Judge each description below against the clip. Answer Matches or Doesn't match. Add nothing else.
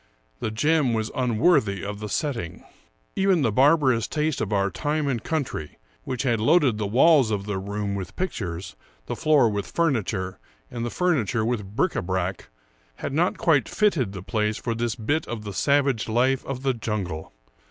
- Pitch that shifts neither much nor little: Doesn't match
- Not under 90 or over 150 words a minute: Doesn't match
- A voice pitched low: Matches